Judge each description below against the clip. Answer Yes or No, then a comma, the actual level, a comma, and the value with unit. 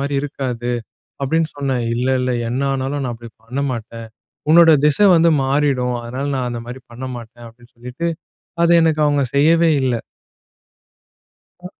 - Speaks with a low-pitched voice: Yes, low, 130 Hz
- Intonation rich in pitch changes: No, average, 3.2 semitones